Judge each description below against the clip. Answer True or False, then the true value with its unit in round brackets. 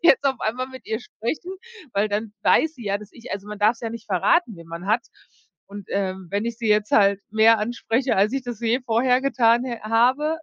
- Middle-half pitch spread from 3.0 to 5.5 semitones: True (3.4 semitones)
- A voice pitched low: False (225 Hz)